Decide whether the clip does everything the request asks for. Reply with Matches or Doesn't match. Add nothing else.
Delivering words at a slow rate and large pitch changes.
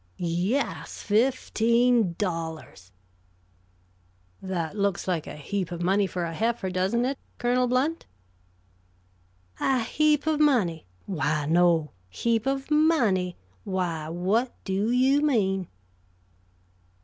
Matches